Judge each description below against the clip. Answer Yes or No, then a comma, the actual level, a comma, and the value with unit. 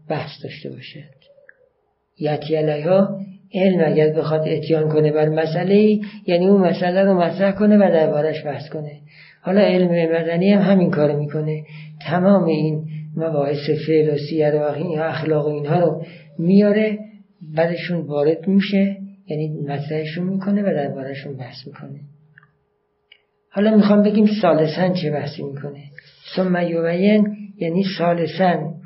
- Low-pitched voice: No, medium, 165 Hz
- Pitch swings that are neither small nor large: Yes, average, 4.0 semitones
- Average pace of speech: Yes, average, 125 wpm